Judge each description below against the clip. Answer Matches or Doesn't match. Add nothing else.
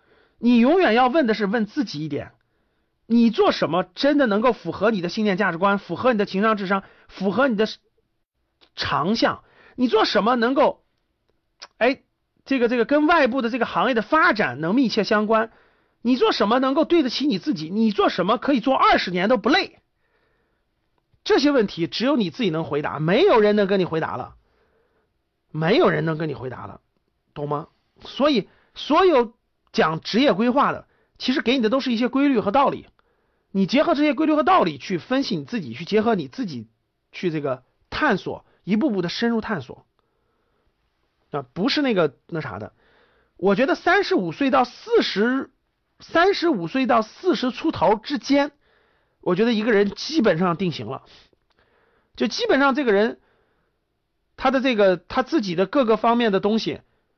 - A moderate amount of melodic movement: Doesn't match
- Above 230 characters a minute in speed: Matches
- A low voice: Doesn't match